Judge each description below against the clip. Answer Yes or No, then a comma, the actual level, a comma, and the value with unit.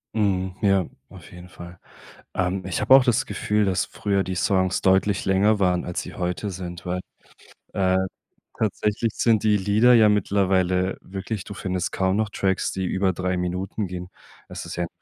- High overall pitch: No, very low, 95 Hz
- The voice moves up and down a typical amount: No, narrow, 2.1 semitones